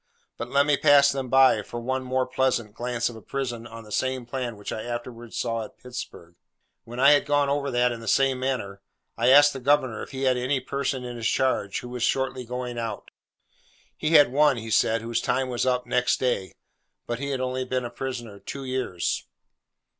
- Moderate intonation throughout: No, narrow, 2.1 semitones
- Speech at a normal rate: No, fast, 215 wpm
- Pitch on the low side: Yes, low, 125 Hz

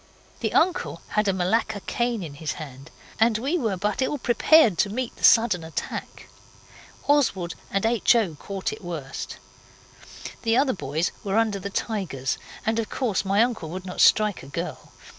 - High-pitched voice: Yes, high, 205 Hz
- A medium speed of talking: Yes, average, 175 wpm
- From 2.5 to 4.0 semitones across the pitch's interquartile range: No, average, 4.8 semitones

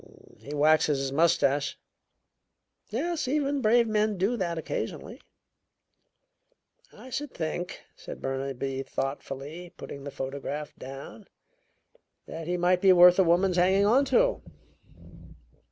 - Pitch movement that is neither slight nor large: No, wide, 7.0 semitones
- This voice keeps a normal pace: No, slow, 120 wpm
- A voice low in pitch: No, medium, 175 Hz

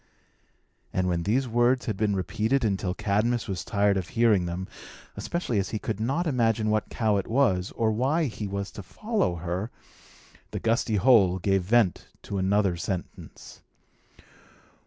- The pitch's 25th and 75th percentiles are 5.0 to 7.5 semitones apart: No, average, 3.8 semitones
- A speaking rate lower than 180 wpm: Yes, average, 155 wpm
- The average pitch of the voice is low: Yes, low, 105 Hz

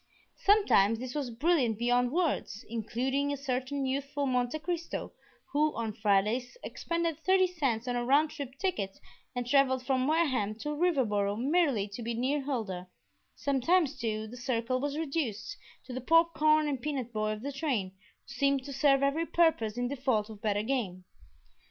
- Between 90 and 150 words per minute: No, average, 165 wpm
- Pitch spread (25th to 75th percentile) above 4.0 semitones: Yes, average, 4.5 semitones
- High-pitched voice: Yes, very high, 260 Hz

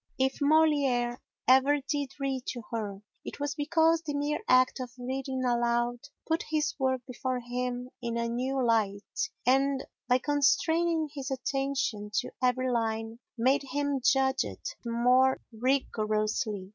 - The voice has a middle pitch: No, very high, 260 Hz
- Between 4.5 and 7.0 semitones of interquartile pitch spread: No, average, 2.9 semitones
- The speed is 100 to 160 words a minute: Yes, average, 140 wpm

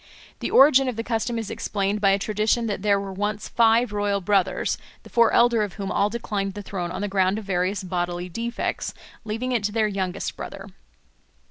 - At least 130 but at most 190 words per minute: No, fast, 205 wpm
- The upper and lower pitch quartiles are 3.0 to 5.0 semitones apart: No, narrow, 2.6 semitones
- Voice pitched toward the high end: Yes, high, 205 Hz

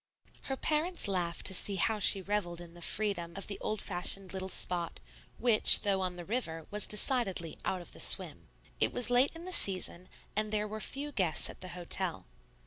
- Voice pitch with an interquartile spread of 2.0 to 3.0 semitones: No, average, 3.6 semitones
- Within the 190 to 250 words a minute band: Yes, average, 200 wpm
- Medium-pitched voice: No, high, 195 Hz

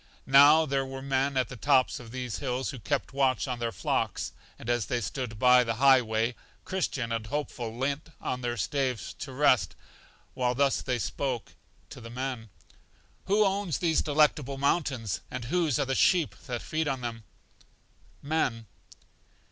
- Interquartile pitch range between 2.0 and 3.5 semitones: Yes, average, 2.9 semitones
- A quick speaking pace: No, average, 170 wpm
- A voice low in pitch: Yes, low, 130 Hz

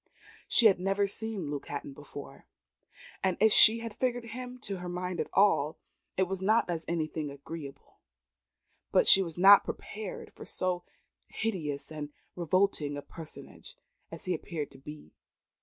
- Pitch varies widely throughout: No, average, 5.0 semitones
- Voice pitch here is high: No, medium, 180 Hz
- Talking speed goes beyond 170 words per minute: No, average, 155 wpm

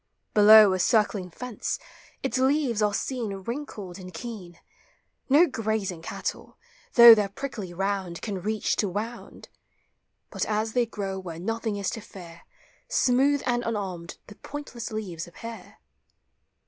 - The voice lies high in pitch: Yes, high, 210 Hz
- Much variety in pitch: No, average, 3.8 semitones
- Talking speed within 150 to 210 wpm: No, slow, 135 wpm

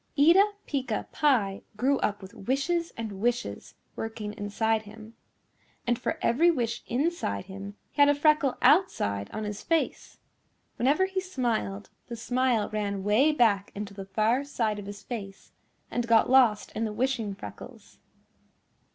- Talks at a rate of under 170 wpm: Yes, average, 150 wpm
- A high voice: Yes, high, 230 Hz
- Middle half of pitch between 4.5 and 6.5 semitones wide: Yes, average, 5.1 semitones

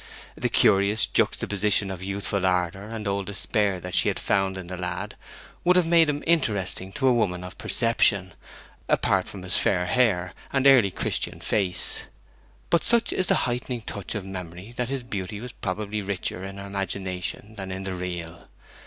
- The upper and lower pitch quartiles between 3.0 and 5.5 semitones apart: Yes, average, 3.6 semitones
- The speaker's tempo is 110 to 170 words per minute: No, average, 180 wpm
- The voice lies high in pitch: No, low, 100 Hz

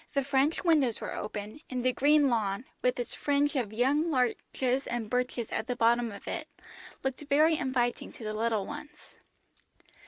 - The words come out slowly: No, average, 175 wpm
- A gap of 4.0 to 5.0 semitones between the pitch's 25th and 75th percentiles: No, average, 3.5 semitones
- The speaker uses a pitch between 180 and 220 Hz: No, very high, 250 Hz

